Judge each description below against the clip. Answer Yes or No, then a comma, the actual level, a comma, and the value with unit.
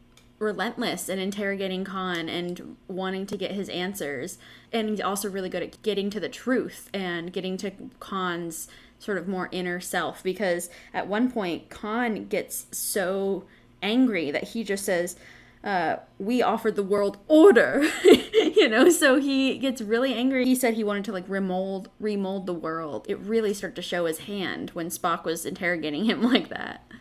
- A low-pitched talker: No, high, 195 Hz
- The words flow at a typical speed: Yes, average, 175 wpm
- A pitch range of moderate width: Yes, average, 4.0 semitones